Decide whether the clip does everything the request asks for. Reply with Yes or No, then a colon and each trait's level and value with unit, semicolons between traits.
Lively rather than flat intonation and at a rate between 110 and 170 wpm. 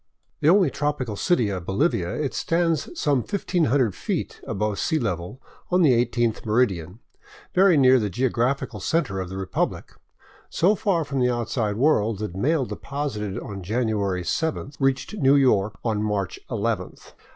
Yes: wide, 6.0 semitones; average, 155 wpm